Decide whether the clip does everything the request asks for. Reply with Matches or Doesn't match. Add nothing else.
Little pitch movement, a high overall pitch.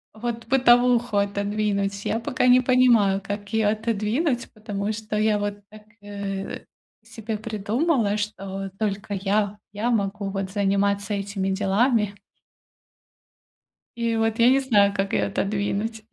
Matches